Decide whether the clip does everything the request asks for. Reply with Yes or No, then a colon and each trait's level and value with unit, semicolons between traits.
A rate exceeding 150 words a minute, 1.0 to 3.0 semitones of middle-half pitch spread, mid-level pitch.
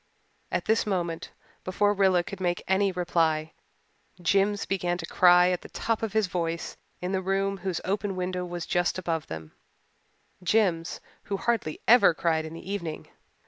Yes: average, 165 wpm; narrow, 2.6 semitones; medium, 180 Hz